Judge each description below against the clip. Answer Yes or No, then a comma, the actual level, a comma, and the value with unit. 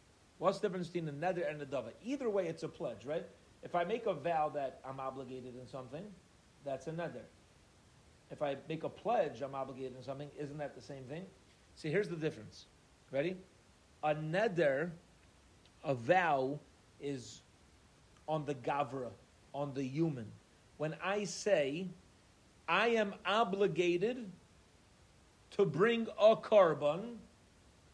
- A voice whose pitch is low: No, medium, 150 Hz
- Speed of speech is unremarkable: Yes, average, 145 wpm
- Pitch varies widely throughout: Yes, wide, 5.8 semitones